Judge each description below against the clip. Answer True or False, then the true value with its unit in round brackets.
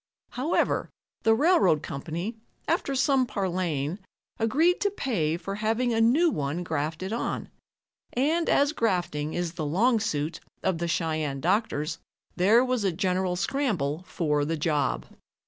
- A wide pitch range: True (7.3 semitones)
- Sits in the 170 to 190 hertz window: True (185 Hz)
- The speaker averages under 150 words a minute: True (140 wpm)